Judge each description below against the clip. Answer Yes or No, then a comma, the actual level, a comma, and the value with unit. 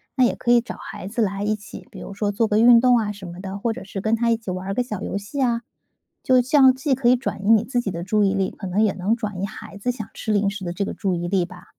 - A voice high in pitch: Yes, high, 210 Hz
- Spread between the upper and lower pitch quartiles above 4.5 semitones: No, average, 3.4 semitones